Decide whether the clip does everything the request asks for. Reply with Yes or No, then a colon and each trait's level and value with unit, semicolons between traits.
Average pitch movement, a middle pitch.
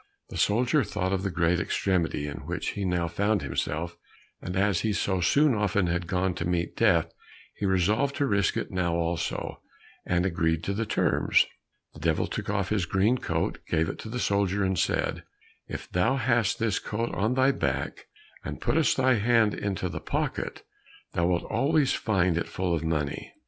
No: average, 4.1 semitones; very low, 95 Hz